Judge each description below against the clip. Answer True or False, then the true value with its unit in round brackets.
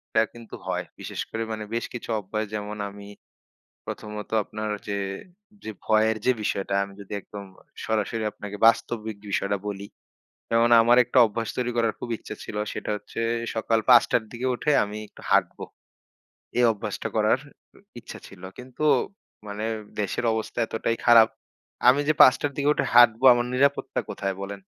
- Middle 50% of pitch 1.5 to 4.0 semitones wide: True (2.5 semitones)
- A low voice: True (110 Hz)